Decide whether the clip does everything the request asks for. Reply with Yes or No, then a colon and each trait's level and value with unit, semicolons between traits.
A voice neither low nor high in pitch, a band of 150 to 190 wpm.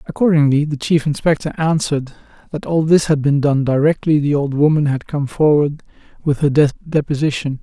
Yes: medium, 150 Hz; average, 165 wpm